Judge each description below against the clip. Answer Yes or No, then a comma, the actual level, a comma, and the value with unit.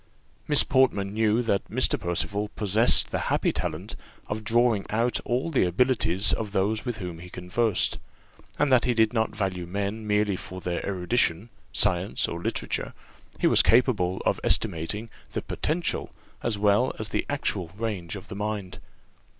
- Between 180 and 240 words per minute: No, average, 160 wpm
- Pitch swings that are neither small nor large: Yes, average, 3.8 semitones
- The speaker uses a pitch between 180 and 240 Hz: No, low, 105 Hz